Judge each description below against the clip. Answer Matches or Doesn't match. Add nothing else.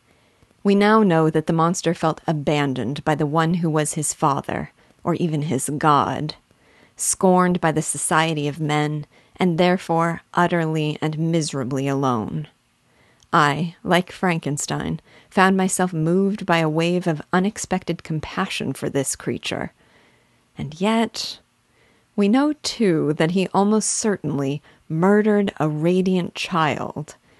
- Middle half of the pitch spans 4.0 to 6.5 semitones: Doesn't match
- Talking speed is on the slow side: Matches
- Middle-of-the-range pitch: Matches